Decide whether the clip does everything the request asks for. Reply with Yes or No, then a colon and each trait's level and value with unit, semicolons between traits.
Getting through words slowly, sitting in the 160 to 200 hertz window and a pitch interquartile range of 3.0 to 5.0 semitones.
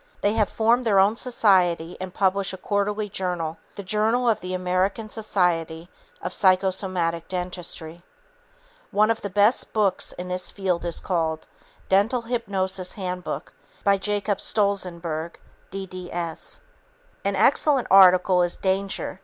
No: slow, 130 wpm; high, 190 Hz; narrow, 2.5 semitones